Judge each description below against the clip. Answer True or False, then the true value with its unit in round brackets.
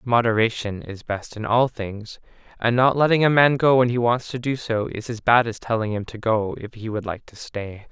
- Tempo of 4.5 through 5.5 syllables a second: True (5.0 syllables/s)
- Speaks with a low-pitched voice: True (115 Hz)